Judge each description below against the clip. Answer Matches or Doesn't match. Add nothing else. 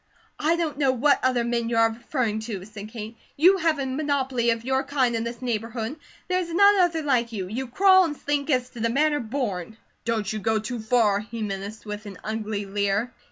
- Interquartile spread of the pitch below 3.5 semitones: Doesn't match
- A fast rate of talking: Matches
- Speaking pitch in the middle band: Doesn't match